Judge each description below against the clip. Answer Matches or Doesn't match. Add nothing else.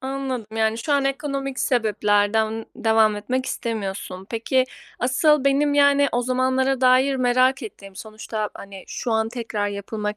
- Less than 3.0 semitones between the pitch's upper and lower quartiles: Doesn't match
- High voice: Matches